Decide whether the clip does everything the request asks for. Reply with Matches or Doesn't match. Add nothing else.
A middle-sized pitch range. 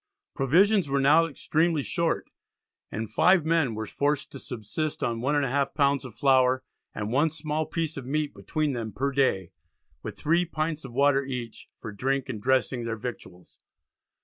Matches